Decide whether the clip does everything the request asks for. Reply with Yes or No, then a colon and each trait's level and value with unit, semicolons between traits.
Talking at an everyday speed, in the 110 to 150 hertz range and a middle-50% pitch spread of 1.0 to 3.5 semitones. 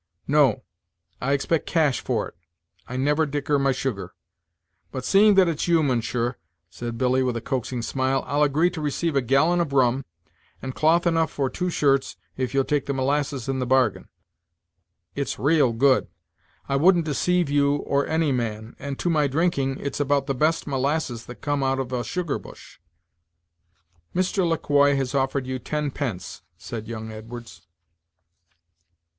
Yes: average, 170 wpm; medium, 140 Hz; average, 2.9 semitones